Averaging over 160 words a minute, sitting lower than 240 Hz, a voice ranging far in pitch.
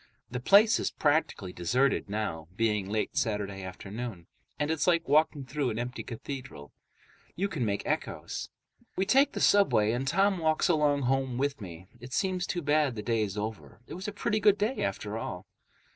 Yes: average, 180 wpm; low, 135 Hz; wide, 7.5 semitones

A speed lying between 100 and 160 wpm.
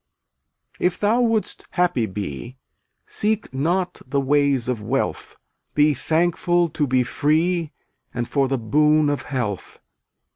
Yes: slow, 135 wpm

